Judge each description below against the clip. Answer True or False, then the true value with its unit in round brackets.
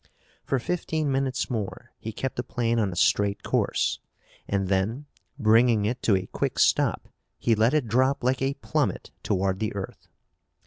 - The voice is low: True (115 Hz)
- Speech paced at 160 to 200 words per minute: True (170 wpm)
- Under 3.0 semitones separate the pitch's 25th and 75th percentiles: False (4.3 semitones)